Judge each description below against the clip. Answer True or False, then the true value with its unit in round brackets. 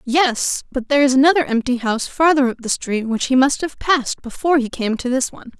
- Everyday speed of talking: False (235 wpm)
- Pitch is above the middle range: True (265 Hz)